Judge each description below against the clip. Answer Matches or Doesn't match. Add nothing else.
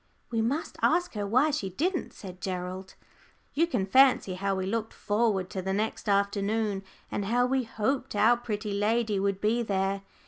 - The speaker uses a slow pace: Doesn't match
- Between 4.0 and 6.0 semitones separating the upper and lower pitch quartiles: Doesn't match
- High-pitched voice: Matches